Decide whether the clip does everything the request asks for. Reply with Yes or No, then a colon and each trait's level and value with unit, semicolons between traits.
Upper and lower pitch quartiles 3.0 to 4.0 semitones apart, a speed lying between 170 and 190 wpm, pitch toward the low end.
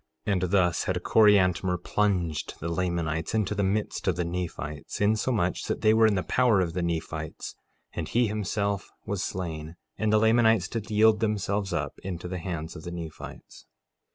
Yes: average, 3.7 semitones; average, 175 wpm; very low, 95 Hz